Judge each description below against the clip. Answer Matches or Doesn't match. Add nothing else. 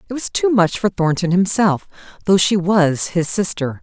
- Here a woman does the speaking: Matches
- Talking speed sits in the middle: Matches